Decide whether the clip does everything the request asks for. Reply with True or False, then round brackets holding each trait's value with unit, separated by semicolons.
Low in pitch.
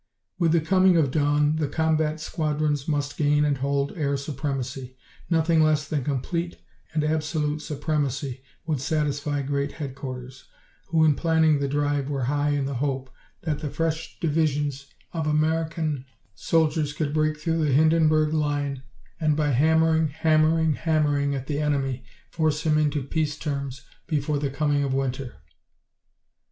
False (150 Hz)